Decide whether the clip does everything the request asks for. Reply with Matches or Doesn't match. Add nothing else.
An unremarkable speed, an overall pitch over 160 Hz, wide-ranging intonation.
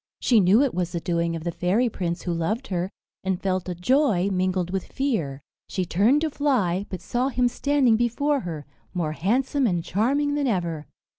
Matches